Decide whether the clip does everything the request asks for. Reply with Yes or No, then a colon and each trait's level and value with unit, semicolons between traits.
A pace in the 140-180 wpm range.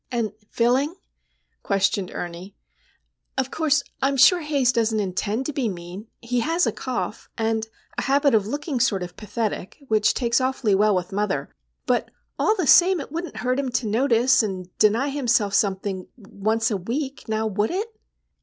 Yes: average, 165 wpm